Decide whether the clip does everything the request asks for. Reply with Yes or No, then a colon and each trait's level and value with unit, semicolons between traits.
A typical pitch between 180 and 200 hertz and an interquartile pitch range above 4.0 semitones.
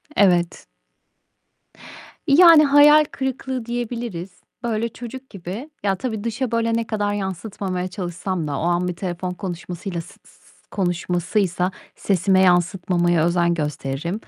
Yes: high, 190 Hz; average, 4.8 semitones